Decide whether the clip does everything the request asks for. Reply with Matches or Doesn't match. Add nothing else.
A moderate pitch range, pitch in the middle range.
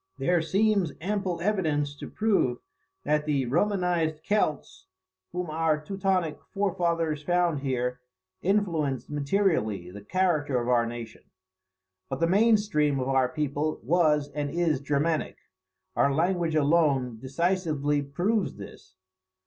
Matches